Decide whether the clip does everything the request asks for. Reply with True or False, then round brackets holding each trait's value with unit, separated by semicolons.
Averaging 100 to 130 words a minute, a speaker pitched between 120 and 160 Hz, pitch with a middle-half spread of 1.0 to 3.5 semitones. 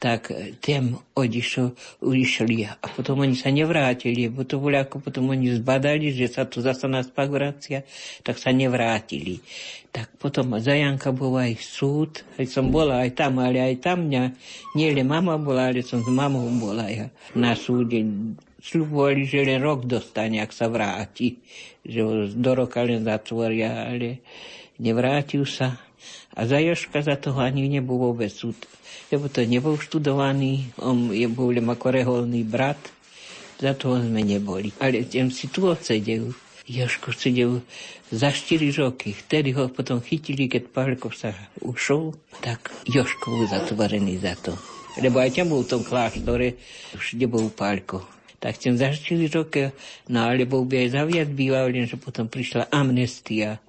False (155 wpm; 130 Hz; 2.8 semitones)